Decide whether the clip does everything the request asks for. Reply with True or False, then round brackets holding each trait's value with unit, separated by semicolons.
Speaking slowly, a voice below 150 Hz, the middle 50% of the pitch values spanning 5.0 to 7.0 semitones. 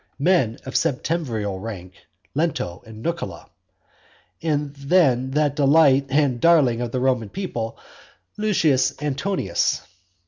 True (110 wpm; 135 Hz; 5.4 semitones)